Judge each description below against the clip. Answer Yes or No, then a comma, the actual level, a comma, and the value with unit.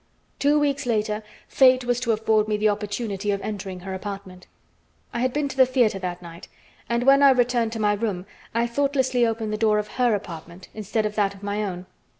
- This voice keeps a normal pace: No, fast, 210 wpm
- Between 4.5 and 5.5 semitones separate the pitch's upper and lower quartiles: No, average, 3.5 semitones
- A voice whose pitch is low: No, high, 215 Hz